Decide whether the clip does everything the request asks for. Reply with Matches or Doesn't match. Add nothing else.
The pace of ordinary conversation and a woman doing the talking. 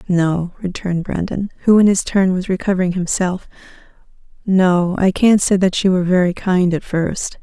Matches